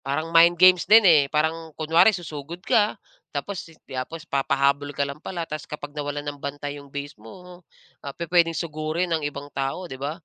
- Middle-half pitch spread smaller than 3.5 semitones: Yes, average, 3.0 semitones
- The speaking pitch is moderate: Yes, medium, 155 Hz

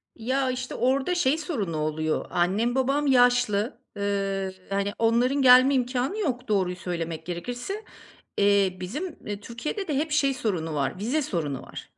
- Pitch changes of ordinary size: No, wide, 6.0 semitones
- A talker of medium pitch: No, high, 235 Hz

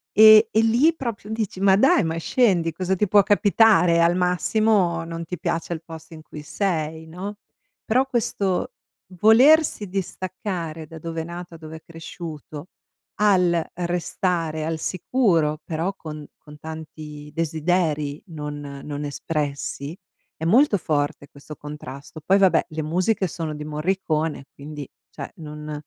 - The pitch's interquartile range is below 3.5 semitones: No, average, 3.9 semitones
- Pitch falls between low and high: Yes, medium, 165 Hz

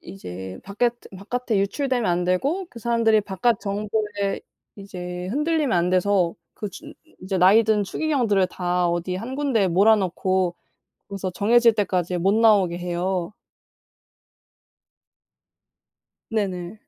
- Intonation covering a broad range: No, average, 3.9 semitones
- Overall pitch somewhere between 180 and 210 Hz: Yes, high, 200 Hz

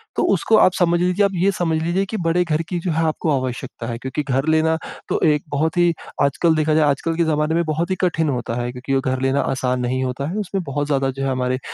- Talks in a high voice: No, medium, 155 Hz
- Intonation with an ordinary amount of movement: Yes, average, 4.3 semitones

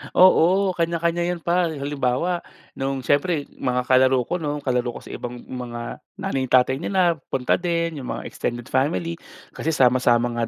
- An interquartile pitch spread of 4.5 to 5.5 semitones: Yes, average, 5.2 semitones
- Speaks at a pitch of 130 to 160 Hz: Yes, medium, 140 Hz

